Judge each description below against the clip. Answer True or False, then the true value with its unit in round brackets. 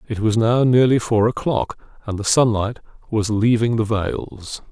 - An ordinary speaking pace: True (165 wpm)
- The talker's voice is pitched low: True (110 Hz)